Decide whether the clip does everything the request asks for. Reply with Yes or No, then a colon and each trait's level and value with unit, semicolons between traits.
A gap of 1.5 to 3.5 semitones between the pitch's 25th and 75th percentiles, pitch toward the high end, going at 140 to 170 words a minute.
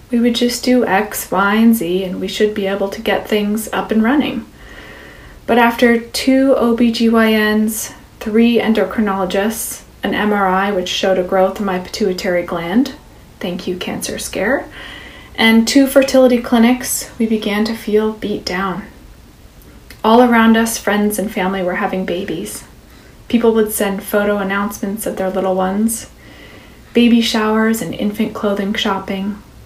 Yes: average, 2.8 semitones; high, 215 Hz; average, 150 wpm